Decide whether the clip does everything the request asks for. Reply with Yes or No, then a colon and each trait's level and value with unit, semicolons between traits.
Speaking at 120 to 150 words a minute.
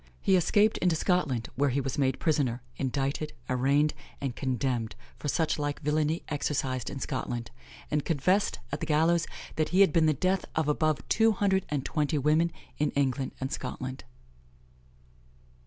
No: average, 160 wpm